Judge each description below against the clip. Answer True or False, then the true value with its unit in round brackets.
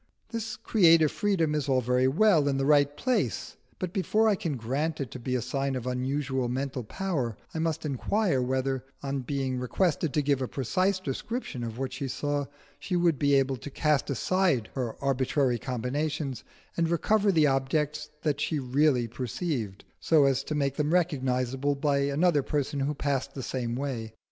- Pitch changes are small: False (3.4 semitones)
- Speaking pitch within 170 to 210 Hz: False (140 Hz)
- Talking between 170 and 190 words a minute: True (180 wpm)